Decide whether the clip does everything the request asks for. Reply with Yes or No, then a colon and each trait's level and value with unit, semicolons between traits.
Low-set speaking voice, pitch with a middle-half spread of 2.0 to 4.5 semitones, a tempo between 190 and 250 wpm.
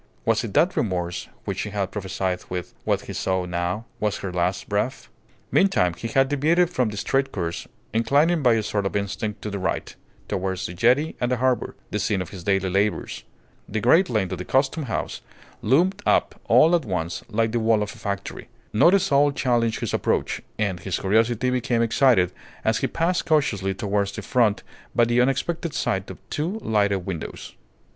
No: low, 110 Hz; wide, 5.4 semitones; average, 195 wpm